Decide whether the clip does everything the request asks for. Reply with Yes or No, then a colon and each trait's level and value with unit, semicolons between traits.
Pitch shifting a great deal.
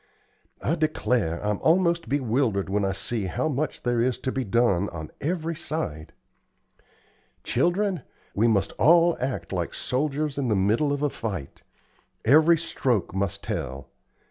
Yes: wide, 7.6 semitones